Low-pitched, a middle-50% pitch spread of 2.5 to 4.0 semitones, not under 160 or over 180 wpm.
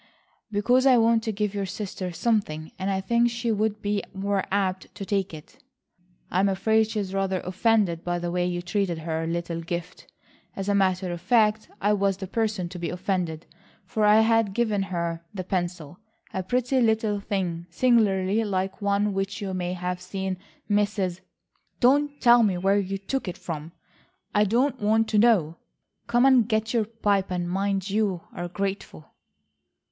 No: high, 195 Hz; average, 3.2 semitones; average, 175 wpm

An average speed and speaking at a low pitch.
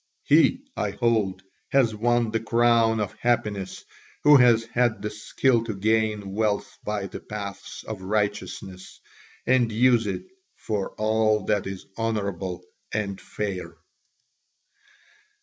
No: slow, 125 wpm; low, 110 Hz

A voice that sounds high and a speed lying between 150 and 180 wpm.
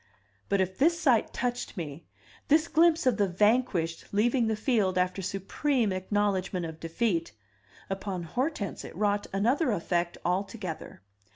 No: high, 200 Hz; slow, 135 wpm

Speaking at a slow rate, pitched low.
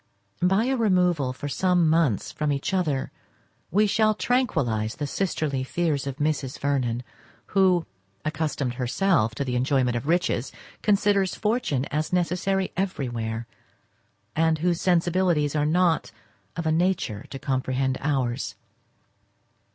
No: slow, 130 wpm; medium, 155 Hz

